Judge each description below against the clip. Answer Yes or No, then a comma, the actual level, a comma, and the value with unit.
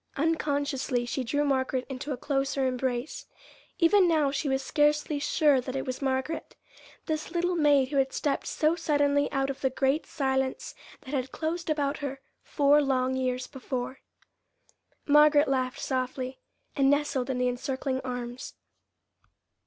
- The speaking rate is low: No, average, 150 wpm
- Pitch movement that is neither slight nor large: No, narrow, 2.2 semitones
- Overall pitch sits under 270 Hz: No, very high, 275 Hz